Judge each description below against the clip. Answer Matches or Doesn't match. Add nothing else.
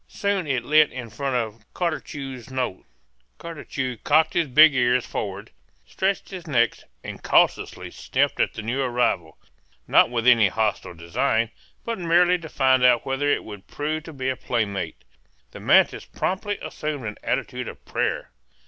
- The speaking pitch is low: Matches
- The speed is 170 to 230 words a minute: Doesn't match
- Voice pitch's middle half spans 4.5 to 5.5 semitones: Matches